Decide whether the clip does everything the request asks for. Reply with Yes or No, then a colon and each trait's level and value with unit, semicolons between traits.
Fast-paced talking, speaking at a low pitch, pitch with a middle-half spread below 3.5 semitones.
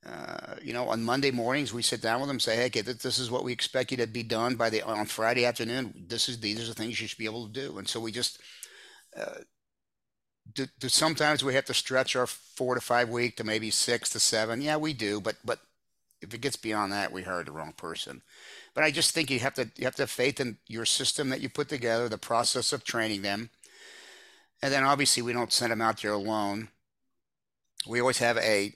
Yes: fast, 240 wpm; low, 120 Hz; average, 2.9 semitones